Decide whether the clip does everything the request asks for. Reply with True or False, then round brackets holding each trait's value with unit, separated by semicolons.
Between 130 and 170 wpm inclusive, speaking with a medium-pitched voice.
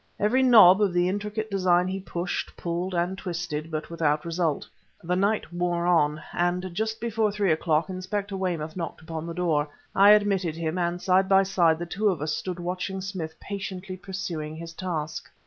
False (180 wpm; 180 Hz)